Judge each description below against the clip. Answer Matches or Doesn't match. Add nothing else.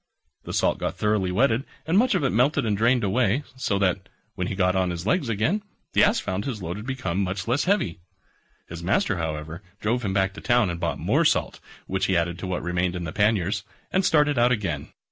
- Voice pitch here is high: Doesn't match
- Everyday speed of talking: Doesn't match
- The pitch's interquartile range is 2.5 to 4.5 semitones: Doesn't match